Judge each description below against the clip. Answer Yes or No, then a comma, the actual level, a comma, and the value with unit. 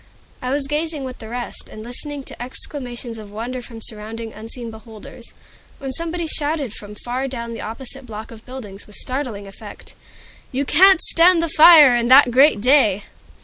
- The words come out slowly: No, average, 175 wpm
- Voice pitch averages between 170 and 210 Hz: No, very high, 250 Hz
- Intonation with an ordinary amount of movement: Yes, average, 4.3 semitones